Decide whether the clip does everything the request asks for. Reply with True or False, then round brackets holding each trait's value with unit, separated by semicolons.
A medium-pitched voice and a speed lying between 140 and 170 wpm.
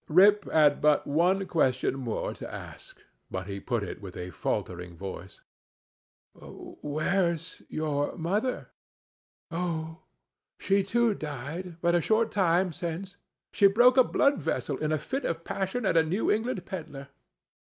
True (165 Hz; 150 wpm)